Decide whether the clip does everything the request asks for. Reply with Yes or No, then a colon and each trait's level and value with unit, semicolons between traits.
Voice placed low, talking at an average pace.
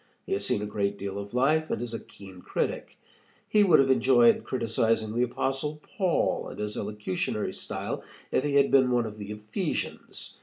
Yes: low, 115 Hz; average, 190 wpm